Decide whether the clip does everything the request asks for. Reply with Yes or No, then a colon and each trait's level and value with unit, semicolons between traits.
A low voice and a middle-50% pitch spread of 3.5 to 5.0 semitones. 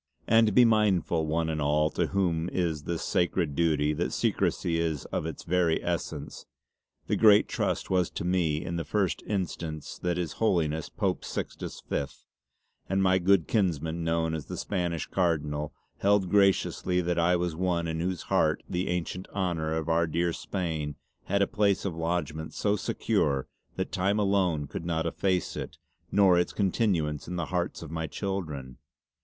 No: very low, 85 Hz; average, 2.7 semitones